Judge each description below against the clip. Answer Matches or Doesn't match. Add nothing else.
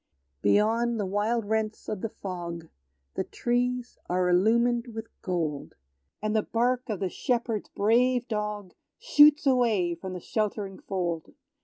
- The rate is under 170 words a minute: Matches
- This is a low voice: Doesn't match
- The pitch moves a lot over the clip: Doesn't match